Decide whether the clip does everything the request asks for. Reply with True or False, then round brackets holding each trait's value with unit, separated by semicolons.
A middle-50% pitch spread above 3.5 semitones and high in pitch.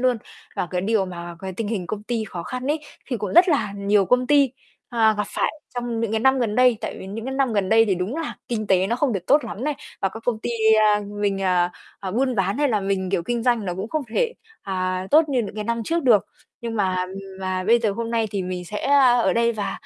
True (4.1 semitones; 220 Hz)